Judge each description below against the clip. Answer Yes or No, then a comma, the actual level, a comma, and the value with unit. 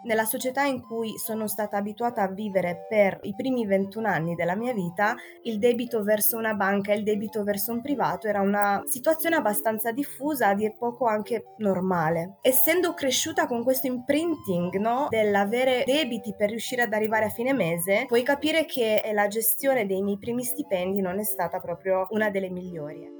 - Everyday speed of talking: No, fast, 180 wpm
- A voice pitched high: Yes, high, 215 Hz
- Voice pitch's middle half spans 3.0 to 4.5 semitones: Yes, average, 3.8 semitones